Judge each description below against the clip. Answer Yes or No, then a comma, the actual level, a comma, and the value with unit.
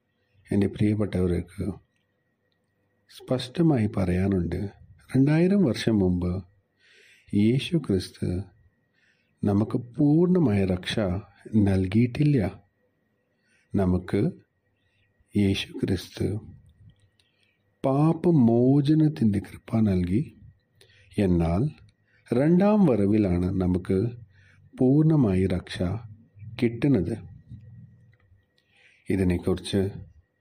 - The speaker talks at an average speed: No, slow, 55 wpm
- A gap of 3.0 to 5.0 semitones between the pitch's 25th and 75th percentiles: Yes, average, 3.6 semitones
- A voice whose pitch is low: Yes, low, 100 Hz